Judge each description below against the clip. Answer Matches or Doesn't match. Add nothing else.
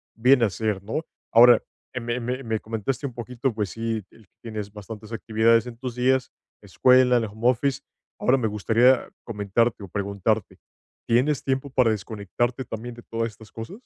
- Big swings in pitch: Doesn't match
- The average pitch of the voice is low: Matches